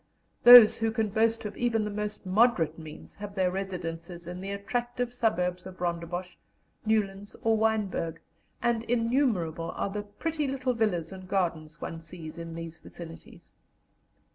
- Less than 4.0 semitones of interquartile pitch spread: No, average, 4.7 semitones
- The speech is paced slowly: No, average, 150 wpm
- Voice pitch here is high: Yes, high, 195 Hz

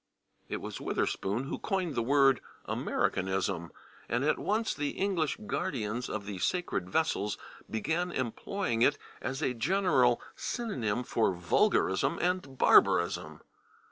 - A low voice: Yes, low, 130 Hz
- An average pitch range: No, wide, 8.7 semitones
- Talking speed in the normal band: No, slow, 130 wpm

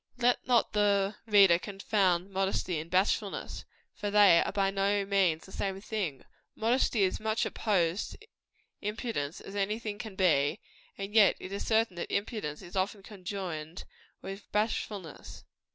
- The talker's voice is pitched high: Yes, high, 195 Hz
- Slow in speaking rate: No, average, 155 wpm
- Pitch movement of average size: No, narrow, 2.3 semitones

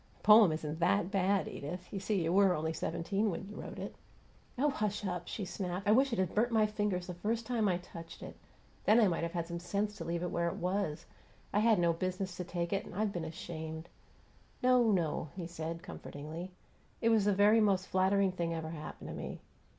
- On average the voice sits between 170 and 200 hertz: Yes, medium, 185 Hz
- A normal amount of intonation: Yes, average, 3.6 semitones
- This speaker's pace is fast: Yes, fast, 225 wpm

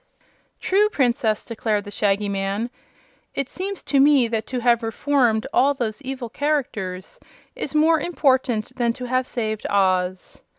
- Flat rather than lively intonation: No, average, 4.5 semitones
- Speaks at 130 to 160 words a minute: Yes, average, 145 wpm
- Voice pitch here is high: Yes, high, 240 Hz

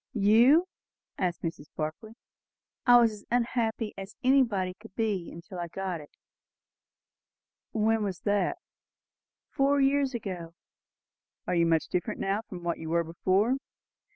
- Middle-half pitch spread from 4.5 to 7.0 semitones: Yes, average, 5.0 semitones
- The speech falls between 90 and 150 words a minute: Yes, slow, 135 wpm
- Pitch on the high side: Yes, high, 200 Hz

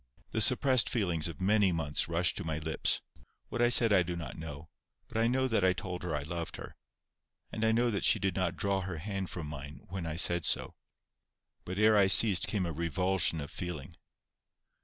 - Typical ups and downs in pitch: Yes, average, 3.8 semitones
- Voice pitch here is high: No, very low, 90 Hz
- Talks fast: Yes, fast, 210 wpm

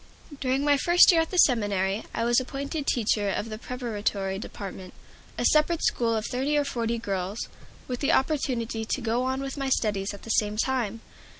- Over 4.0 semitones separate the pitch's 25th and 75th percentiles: Yes, average, 4.5 semitones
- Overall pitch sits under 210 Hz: No, high, 235 Hz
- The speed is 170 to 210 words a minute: Yes, average, 190 wpm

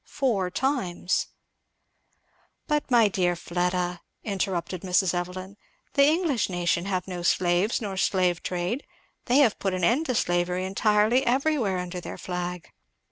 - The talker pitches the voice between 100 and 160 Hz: No, medium, 185 Hz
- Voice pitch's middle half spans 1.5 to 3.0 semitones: No, average, 4.8 semitones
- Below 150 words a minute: Yes, slow, 135 wpm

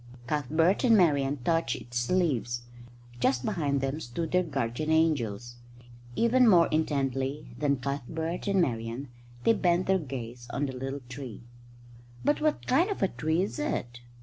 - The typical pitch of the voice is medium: Yes, medium, 145 Hz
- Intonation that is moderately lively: No, wide, 5.7 semitones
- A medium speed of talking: Yes, average, 150 wpm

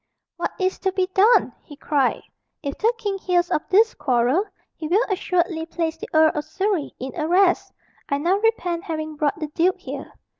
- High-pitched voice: Yes, very high, 345 Hz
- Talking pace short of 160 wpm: No, average, 185 wpm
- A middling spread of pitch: Yes, average, 4.0 semitones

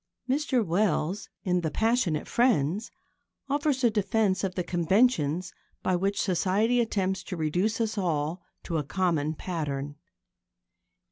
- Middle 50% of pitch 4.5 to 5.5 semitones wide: Yes, average, 5.1 semitones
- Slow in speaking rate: Yes, slow, 130 wpm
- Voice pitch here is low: No, medium, 185 Hz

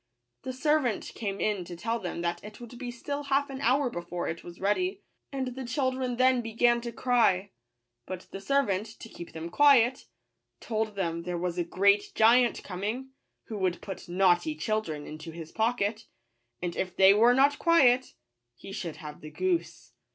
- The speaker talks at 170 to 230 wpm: Yes, average, 185 wpm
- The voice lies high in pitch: Yes, high, 220 Hz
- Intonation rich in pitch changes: Yes, wide, 6.1 semitones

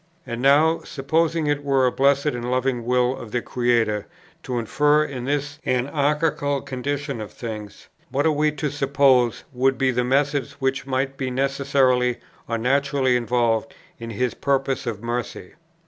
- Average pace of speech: Yes, average, 160 wpm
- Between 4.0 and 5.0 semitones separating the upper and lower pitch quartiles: No, narrow, 2.5 semitones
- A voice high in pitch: No, low, 135 Hz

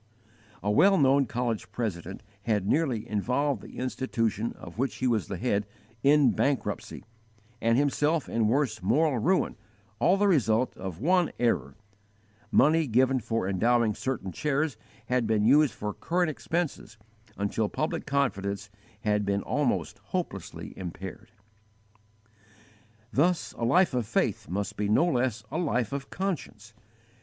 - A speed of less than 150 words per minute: Yes, average, 140 wpm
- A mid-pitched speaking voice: No, low, 120 Hz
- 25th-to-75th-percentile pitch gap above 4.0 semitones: Yes, wide, 5.5 semitones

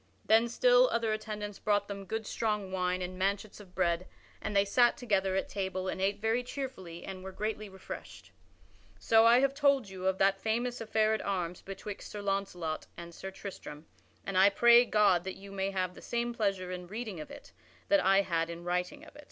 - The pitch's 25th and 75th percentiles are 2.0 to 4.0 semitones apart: Yes, average, 3.0 semitones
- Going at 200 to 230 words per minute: Yes, fast, 205 wpm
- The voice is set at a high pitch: Yes, high, 200 Hz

